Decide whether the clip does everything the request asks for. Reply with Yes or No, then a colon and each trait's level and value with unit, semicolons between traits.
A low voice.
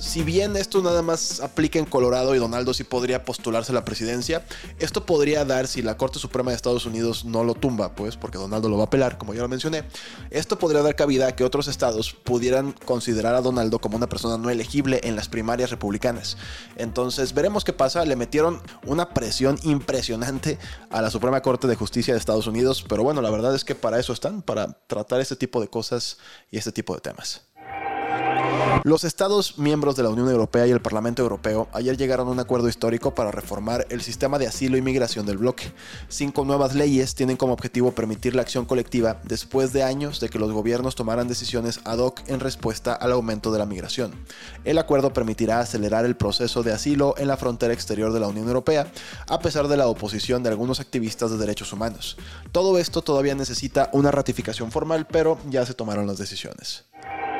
Yes: low, 125 Hz